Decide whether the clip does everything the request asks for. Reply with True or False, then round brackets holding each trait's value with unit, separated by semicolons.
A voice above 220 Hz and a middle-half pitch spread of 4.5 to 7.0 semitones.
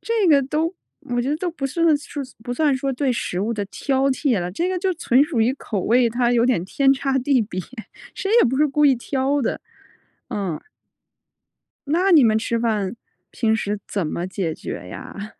True (255 Hz; 4.8 semitones)